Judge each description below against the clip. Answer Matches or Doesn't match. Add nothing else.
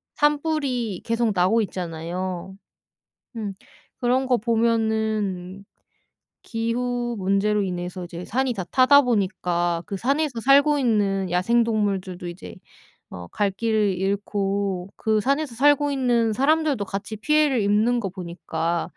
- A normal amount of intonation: Matches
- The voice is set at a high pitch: Matches